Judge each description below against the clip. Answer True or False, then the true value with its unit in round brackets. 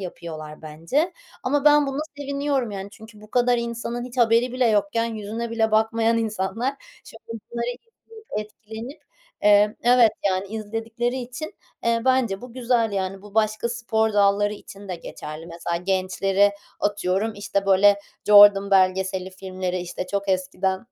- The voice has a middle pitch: False (215 Hz)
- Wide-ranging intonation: False (3.5 semitones)